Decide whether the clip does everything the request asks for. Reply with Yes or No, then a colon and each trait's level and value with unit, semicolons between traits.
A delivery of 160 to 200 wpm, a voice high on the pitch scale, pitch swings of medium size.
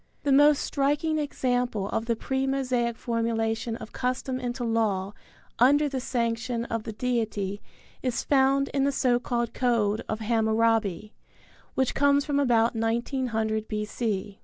No: average, 140 wpm; high, 235 Hz; average, 3.0 semitones